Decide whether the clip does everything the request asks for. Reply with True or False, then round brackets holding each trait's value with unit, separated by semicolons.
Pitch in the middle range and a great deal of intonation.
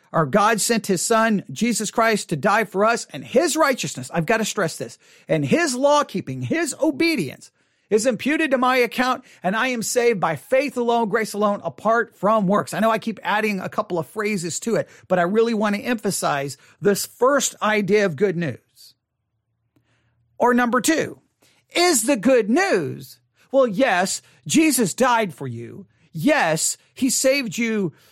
False (215 Hz; 6.8 semitones)